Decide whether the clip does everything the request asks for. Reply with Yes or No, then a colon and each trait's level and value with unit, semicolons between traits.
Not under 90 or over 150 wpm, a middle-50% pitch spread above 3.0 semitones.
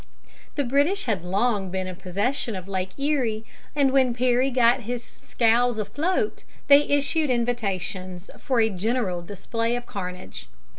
Yes: average, 145 wpm; average, 5.2 semitones